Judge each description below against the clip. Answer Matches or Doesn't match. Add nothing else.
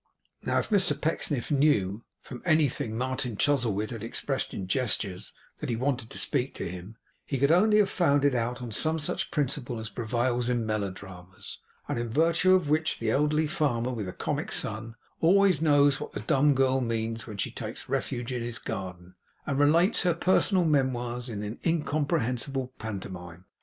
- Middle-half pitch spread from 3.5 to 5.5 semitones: Matches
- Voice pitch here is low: Matches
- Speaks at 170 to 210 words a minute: Matches